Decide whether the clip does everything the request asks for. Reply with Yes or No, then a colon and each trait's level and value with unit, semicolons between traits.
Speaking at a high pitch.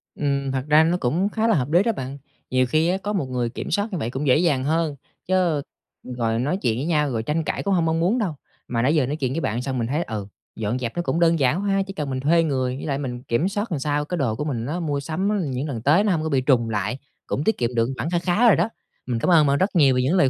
No: medium, 145 Hz